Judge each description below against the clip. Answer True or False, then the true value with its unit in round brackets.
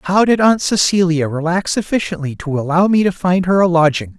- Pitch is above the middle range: False (175 Hz)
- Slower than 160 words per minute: False (200 wpm)